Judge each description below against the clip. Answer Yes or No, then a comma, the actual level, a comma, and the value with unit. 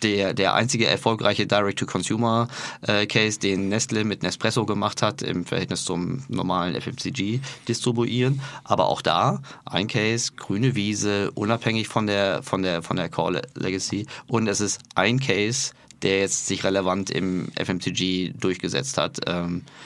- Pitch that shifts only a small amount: No, average, 3.6 semitones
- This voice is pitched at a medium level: No, low, 105 Hz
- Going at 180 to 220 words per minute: No, average, 140 wpm